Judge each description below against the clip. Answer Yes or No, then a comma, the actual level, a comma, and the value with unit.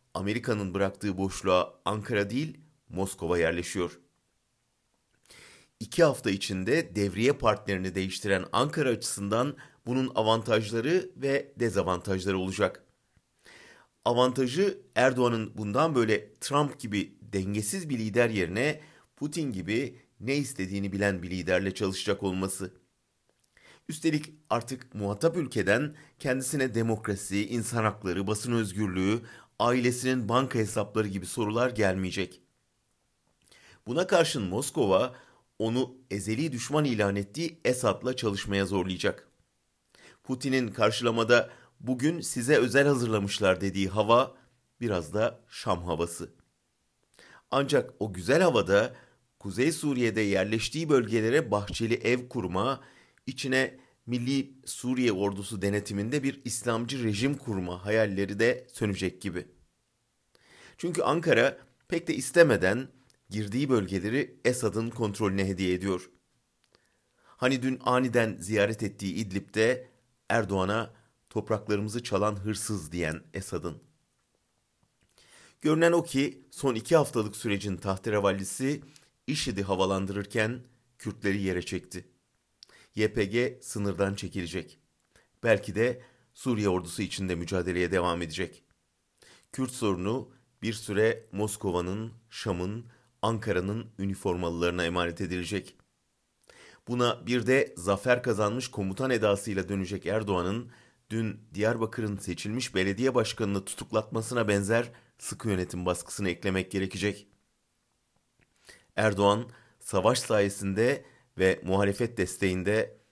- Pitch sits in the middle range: No, low, 110 Hz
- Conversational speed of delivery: No, slow, 100 wpm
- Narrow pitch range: No, average, 4.2 semitones